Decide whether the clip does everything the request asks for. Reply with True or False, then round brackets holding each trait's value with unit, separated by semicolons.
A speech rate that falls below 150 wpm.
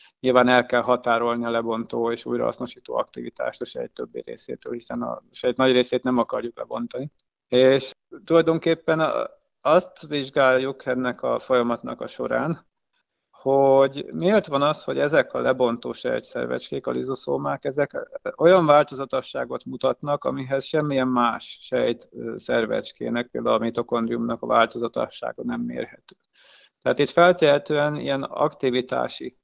True (125 wpm)